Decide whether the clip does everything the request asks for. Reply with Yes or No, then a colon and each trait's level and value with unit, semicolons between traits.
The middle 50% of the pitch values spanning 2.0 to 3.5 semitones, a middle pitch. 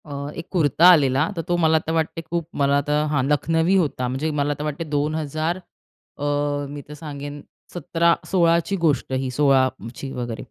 Yes: average, 2.7 semitones; medium, 150 Hz